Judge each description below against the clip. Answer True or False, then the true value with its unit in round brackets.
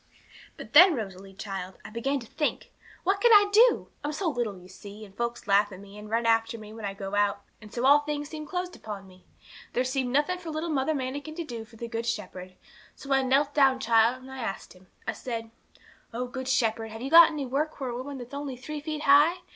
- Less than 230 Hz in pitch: False (250 Hz)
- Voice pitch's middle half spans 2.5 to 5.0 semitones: False (5.4 semitones)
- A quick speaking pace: True (240 wpm)